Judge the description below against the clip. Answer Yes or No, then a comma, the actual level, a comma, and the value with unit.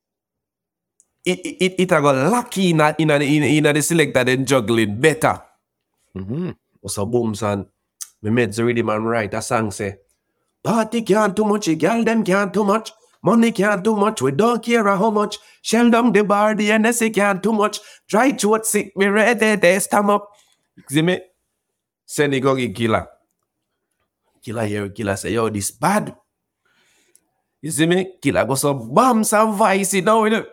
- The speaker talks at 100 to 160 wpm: No, average, 180 wpm